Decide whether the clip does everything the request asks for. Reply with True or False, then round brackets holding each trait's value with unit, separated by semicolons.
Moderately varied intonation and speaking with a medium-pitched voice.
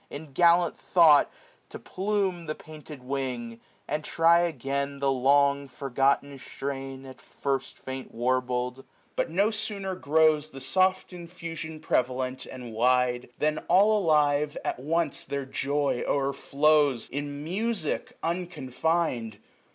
True (4.0 semitones; 145 Hz)